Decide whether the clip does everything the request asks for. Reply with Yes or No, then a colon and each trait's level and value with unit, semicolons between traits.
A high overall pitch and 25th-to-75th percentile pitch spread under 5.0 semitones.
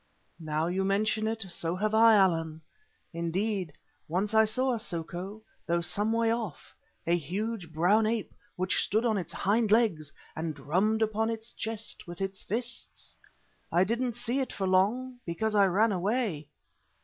Yes: high, 205 Hz; average, 4.3 semitones